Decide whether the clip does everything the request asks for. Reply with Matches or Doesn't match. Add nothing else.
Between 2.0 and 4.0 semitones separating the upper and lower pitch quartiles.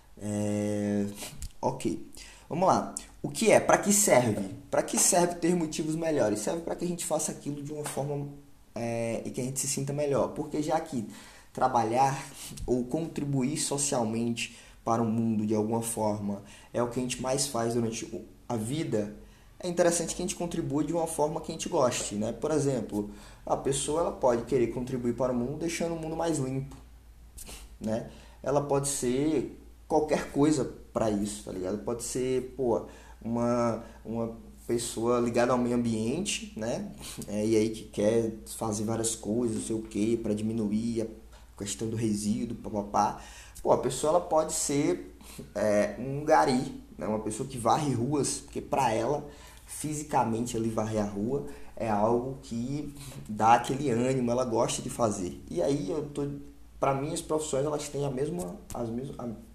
Doesn't match